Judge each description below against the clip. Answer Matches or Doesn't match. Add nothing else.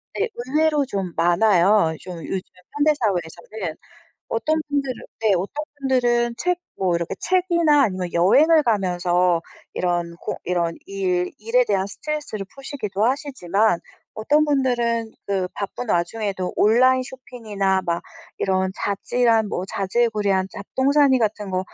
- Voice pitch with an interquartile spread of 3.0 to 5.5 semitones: Doesn't match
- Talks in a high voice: Matches